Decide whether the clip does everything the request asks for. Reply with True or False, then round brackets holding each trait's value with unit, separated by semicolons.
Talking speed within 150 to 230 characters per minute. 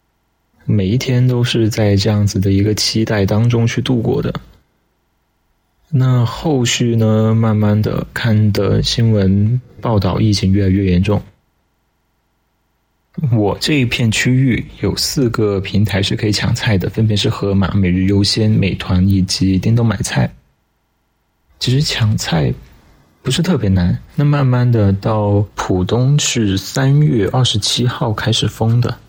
True (210 characters per minute)